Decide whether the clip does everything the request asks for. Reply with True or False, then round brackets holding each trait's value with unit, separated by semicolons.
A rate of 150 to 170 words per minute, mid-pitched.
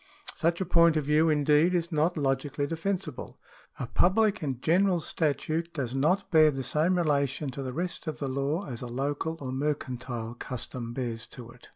False (185 wpm; 150 Hz)